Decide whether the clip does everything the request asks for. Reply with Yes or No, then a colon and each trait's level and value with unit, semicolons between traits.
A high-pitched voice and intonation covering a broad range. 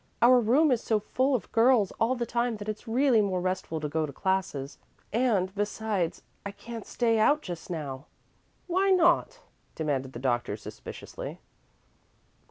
Yes: high, 215 Hz; wide, 6.6 semitones